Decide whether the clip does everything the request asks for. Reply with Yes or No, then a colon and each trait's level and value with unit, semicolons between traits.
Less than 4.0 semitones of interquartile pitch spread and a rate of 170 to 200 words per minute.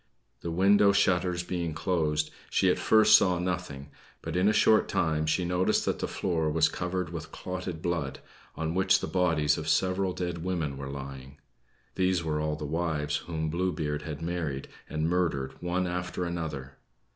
Yes: average, 2.9 semitones; average, 175 wpm